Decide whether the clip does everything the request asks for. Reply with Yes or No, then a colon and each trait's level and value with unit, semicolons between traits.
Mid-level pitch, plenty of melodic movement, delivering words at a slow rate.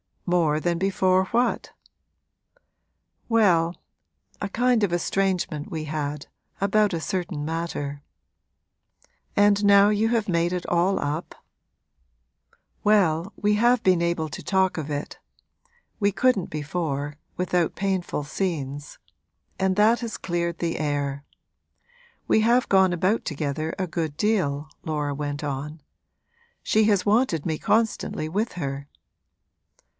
No: medium, 175 Hz; average, 4.9 semitones; slow, 125 wpm